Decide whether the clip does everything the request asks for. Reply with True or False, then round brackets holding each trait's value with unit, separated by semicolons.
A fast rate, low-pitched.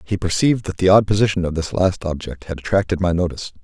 True (230 wpm; 90 Hz)